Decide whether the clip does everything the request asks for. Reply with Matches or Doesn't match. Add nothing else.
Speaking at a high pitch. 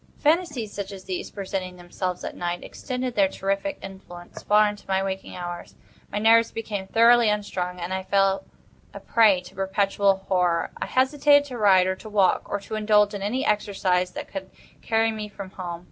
Matches